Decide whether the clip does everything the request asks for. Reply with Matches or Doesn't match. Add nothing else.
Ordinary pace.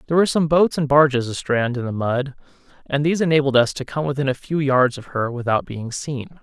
Doesn't match